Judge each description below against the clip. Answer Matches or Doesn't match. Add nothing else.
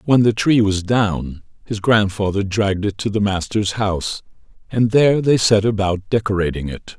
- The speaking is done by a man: Matches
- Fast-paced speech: Doesn't match